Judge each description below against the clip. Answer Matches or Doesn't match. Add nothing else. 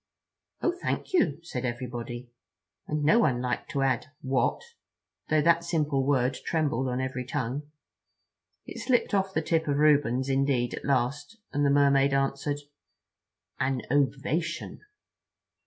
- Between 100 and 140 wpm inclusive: Matches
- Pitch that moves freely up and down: Doesn't match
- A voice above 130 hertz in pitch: Matches